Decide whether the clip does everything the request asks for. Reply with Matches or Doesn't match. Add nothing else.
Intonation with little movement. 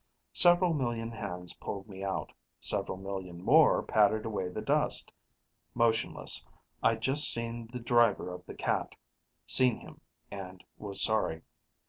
Doesn't match